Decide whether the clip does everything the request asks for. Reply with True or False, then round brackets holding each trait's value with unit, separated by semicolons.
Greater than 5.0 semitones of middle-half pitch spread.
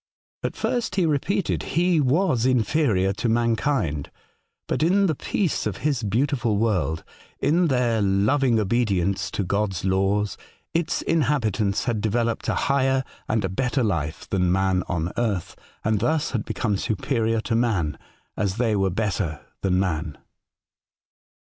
True (5.5 semitones)